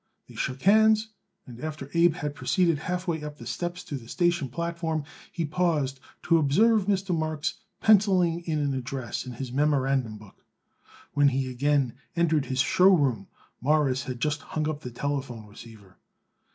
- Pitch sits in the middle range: Yes, medium, 150 Hz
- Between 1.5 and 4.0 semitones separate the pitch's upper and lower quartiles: No, average, 4.5 semitones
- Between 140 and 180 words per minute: Yes, average, 165 wpm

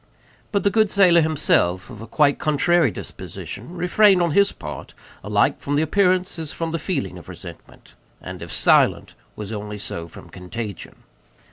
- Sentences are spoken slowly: No, average, 165 wpm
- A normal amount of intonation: No, wide, 8.3 semitones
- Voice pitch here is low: No, medium, 155 Hz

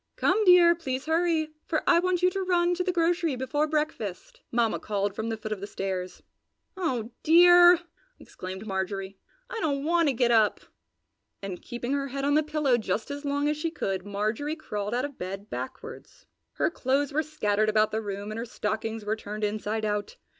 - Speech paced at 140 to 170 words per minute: No, average, 195 wpm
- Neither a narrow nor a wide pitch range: No, wide, 7.1 semitones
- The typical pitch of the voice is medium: No, very high, 255 Hz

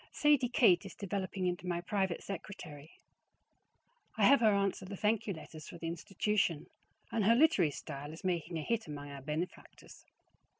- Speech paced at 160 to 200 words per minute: Yes, average, 170 wpm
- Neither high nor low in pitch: Yes, medium, 180 Hz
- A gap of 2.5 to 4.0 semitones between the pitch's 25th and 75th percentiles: No, average, 4.5 semitones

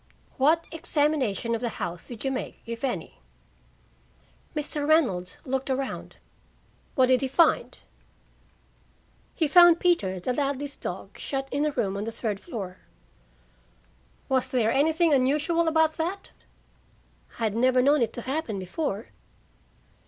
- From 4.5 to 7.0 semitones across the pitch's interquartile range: Yes, average, 5.0 semitones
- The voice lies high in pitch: Yes, very high, 270 Hz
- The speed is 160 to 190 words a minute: No, slow, 135 wpm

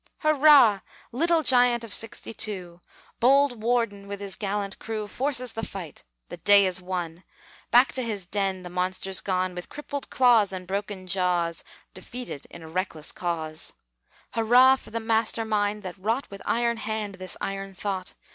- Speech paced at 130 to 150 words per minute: No, average, 160 wpm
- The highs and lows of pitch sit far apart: No, average, 4.2 semitones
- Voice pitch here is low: No, high, 205 Hz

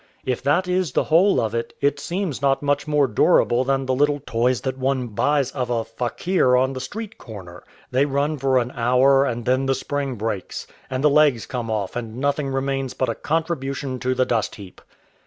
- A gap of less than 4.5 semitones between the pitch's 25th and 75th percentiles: Yes, average, 2.8 semitones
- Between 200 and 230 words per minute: Yes, fast, 205 wpm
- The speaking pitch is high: No, low, 130 Hz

